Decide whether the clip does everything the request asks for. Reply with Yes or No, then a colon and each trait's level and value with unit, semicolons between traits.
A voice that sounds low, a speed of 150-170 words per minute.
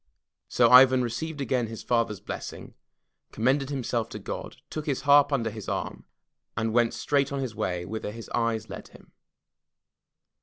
Yes: low, 120 Hz; average, 160 wpm